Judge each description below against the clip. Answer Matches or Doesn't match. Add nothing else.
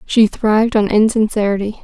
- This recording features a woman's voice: Matches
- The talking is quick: Doesn't match